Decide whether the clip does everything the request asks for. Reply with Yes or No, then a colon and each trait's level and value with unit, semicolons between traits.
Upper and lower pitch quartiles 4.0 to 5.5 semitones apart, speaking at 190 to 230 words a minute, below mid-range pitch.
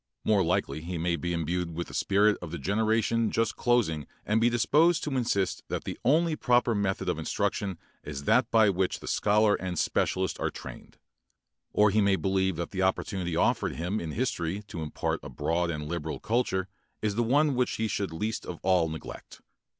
Yes: average, 4.6 semitones; average, 195 wpm; very low, 95 Hz